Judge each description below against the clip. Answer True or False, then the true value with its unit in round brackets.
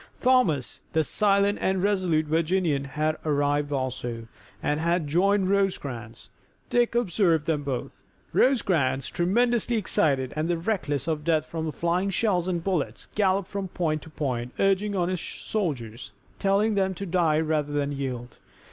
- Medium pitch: True (165 Hz)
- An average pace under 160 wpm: True (145 wpm)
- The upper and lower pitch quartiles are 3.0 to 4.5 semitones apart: False (5.1 semitones)